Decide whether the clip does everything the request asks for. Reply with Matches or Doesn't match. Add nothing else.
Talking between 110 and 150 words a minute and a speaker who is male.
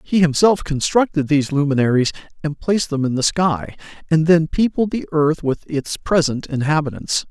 Doesn't match